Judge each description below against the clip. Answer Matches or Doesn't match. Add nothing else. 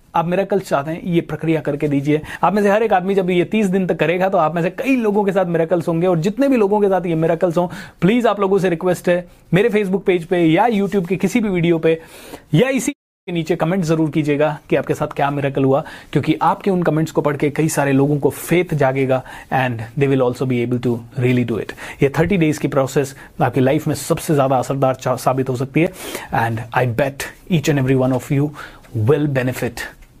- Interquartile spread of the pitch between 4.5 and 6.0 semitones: Matches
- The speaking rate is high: Matches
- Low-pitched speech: Doesn't match